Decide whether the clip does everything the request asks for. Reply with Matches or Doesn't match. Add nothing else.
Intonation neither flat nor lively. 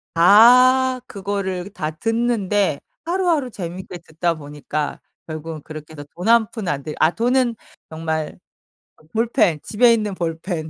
Doesn't match